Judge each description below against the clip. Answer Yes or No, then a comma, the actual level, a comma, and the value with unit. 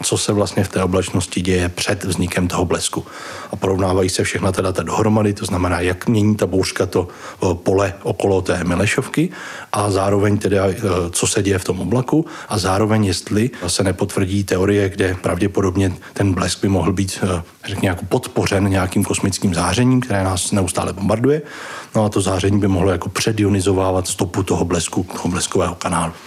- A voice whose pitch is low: Yes, very low, 95 Hz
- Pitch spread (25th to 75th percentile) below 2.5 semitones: Yes, narrow, 1.9 semitones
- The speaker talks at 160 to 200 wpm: Yes, fast, 170 wpm